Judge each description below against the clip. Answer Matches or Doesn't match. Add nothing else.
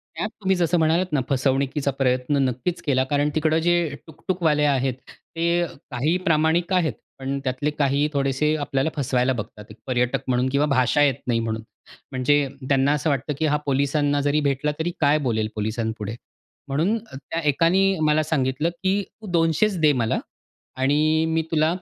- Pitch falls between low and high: Matches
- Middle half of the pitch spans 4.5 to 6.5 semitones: Doesn't match